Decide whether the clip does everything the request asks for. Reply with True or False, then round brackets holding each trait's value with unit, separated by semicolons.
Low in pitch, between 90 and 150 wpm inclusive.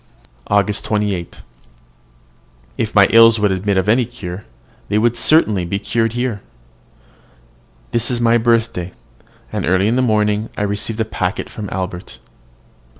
True (105 Hz; 145 wpm)